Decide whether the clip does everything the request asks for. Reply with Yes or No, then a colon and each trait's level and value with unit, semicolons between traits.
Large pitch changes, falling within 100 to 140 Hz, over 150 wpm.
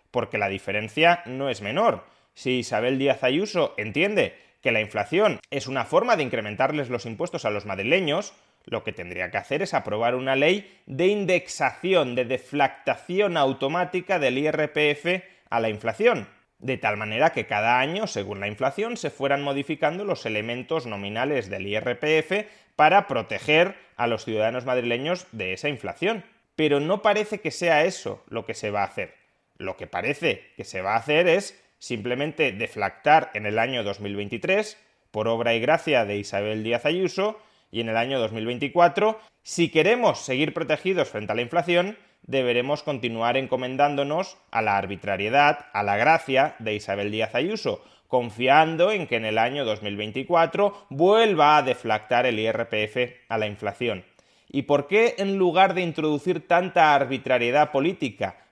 Yes: wide, 7.2 semitones; low, 135 Hz; average, 160 wpm